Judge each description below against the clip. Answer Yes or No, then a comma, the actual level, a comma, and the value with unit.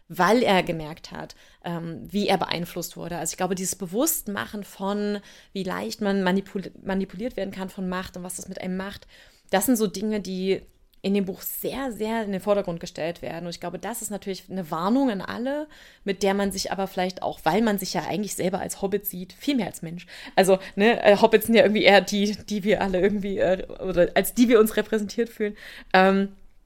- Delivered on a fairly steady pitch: Yes, narrow, 2.2 semitones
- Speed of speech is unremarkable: No, fast, 205 wpm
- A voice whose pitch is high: Yes, high, 195 Hz